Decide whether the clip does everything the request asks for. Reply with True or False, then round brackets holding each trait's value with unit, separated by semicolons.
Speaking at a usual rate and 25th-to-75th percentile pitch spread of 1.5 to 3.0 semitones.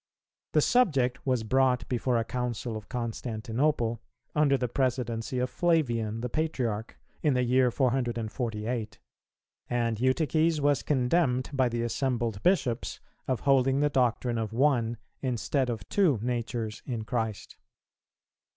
False (130 wpm; 2.7 semitones)